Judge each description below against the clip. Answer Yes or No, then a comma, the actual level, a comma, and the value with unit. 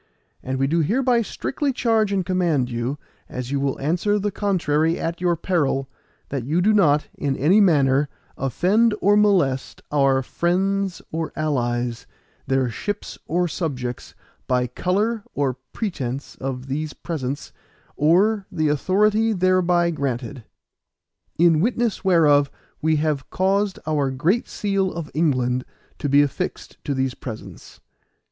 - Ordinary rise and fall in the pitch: No, wide, 6.1 semitones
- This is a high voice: No, medium, 155 Hz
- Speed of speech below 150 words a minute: Yes, average, 140 wpm